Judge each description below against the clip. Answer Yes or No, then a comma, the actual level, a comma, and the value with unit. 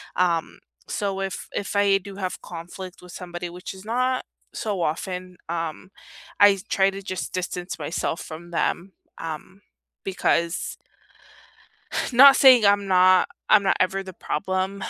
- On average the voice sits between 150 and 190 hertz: Yes, medium, 185 Hz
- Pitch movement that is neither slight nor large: No, narrow, 2.1 semitones